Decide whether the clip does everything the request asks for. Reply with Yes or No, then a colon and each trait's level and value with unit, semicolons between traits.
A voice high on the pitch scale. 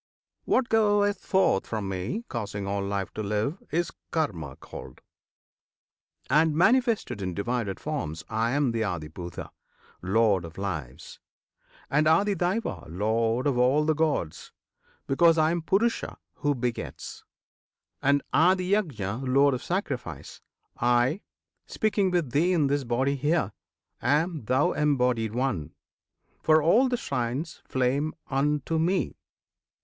No: low, 135 Hz